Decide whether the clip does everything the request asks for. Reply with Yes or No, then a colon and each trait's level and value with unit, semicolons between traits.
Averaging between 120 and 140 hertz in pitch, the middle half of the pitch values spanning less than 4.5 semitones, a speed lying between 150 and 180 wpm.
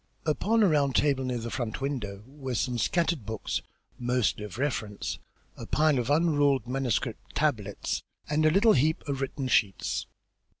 Yes: low, 135 Hz; average, 3.8 semitones; average, 160 wpm